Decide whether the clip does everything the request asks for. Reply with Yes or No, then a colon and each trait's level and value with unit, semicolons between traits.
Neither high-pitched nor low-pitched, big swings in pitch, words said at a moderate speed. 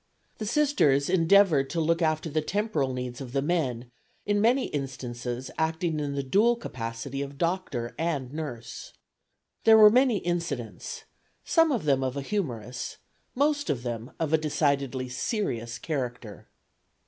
Yes: medium, 145 Hz; wide, 6.5 semitones; average, 150 wpm